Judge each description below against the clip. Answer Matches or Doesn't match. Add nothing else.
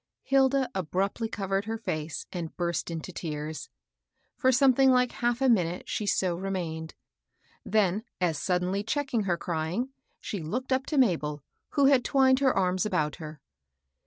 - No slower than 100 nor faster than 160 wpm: Matches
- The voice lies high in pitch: Matches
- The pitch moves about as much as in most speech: Doesn't match